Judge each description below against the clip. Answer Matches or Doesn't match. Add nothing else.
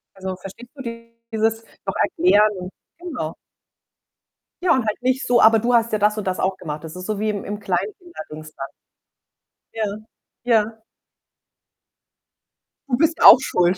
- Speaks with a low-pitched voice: Doesn't match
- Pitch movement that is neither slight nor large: Matches